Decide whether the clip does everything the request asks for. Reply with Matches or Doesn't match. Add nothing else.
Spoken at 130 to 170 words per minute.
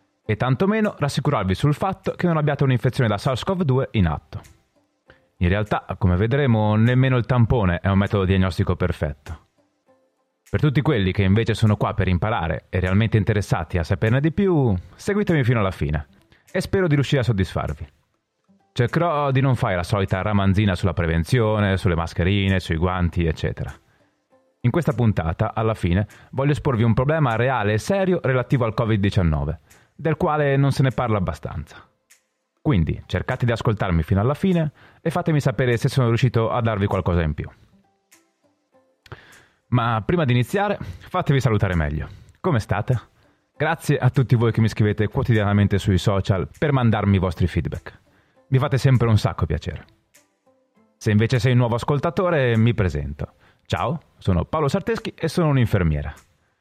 Matches